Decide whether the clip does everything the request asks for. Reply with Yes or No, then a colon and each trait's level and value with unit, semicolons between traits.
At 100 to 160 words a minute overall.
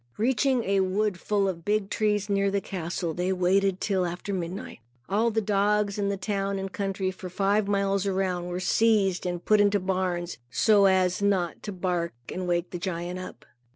No: average, 190 wpm